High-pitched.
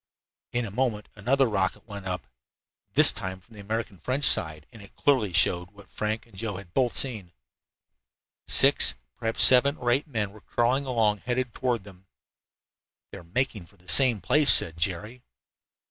No: low, 105 Hz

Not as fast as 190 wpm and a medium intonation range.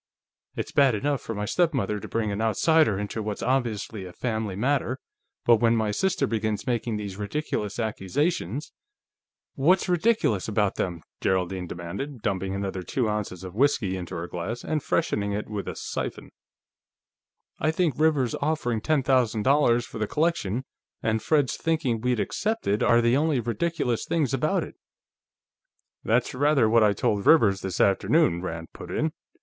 No: average, 165 wpm; wide, 5.8 semitones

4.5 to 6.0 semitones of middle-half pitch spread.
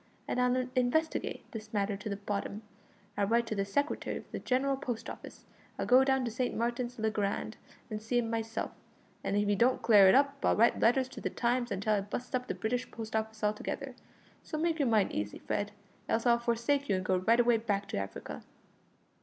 No: average, 3.3 semitones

